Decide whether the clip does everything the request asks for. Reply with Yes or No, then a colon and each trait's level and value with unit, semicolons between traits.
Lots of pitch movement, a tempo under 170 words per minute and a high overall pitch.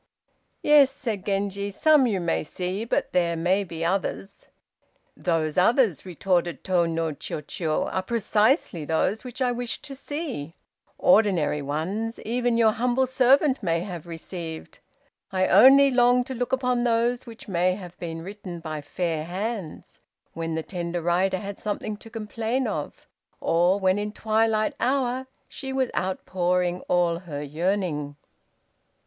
Yes: wide, 5.7 semitones; average, 145 wpm; high, 195 Hz